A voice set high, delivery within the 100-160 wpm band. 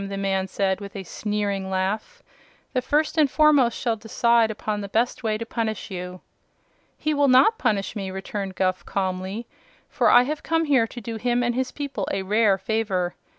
No: high, 220 Hz; average, 190 wpm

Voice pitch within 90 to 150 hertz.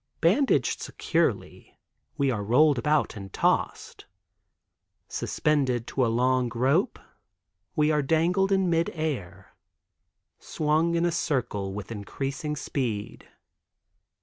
Yes: medium, 140 Hz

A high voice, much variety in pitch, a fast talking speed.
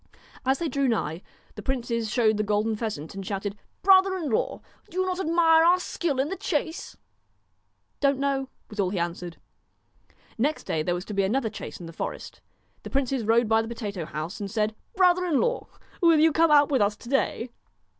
Yes: high, 240 Hz; wide, 7.4 semitones; fast, 215 wpm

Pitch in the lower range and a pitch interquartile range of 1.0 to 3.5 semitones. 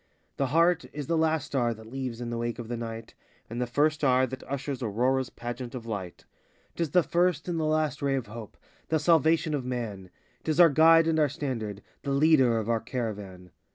No: low, 130 Hz; average, 5.0 semitones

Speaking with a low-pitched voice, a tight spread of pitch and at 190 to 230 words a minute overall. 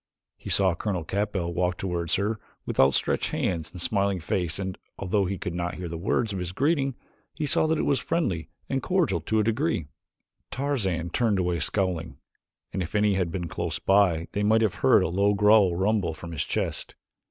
No: very low, 95 Hz; average, 3.9 semitones; average, 200 wpm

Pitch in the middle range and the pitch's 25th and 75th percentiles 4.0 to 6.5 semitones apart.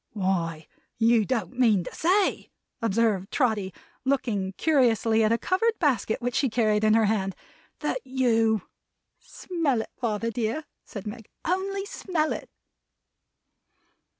No: high, 230 Hz; average, 4.3 semitones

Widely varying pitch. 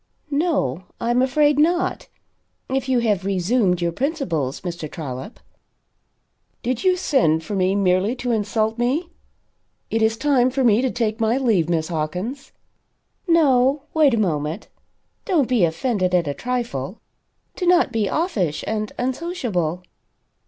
Yes: wide, 6.8 semitones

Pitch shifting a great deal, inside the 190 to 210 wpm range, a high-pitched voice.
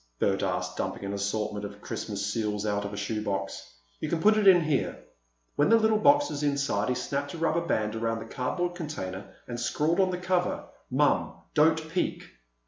No: wide, 8.7 semitones; average, 195 wpm; low, 125 Hz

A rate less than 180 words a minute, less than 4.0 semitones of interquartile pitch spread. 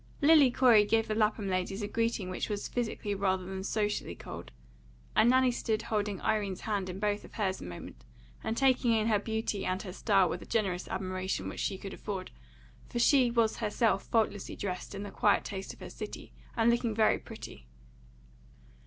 No: average, 190 wpm; average, 2.8 semitones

